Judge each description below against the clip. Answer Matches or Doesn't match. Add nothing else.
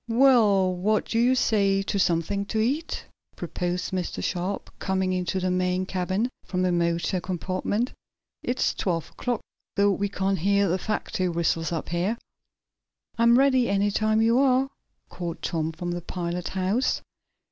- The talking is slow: Doesn't match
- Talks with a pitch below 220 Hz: Matches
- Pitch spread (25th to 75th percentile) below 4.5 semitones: Matches